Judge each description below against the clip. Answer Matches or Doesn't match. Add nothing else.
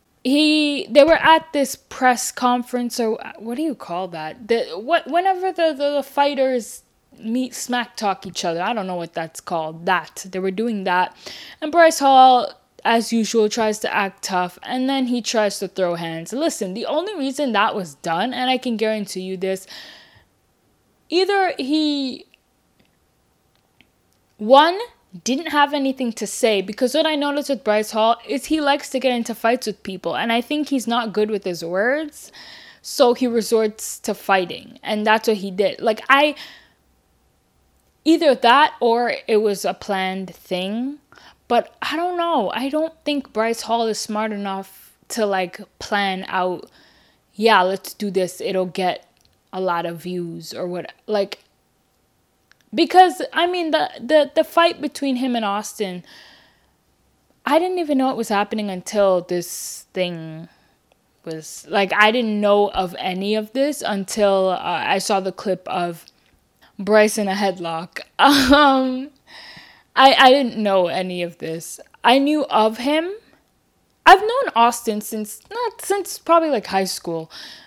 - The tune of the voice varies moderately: Doesn't match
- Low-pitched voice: Doesn't match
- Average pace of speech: Matches